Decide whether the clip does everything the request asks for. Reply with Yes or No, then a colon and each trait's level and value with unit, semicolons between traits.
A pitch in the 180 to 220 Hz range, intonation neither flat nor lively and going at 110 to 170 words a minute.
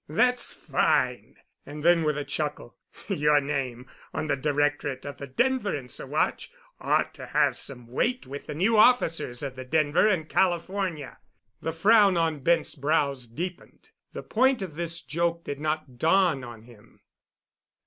No: medium, 155 Hz; average, 4.0 semitones; average, 160 wpm